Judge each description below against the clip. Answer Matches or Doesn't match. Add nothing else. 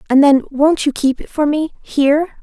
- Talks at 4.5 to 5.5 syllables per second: Matches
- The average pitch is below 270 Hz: Doesn't match